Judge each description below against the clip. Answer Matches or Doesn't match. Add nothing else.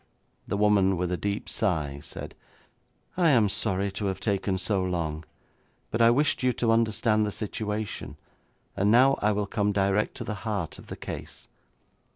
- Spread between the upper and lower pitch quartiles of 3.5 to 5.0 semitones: Doesn't match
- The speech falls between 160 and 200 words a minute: Matches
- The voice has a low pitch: Matches